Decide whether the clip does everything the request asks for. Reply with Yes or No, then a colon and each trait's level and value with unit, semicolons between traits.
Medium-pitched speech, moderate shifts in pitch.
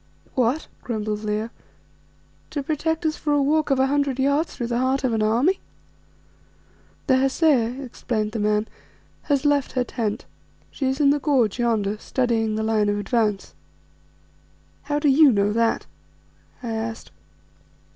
No: very high, 250 Hz; average, 4.4 semitones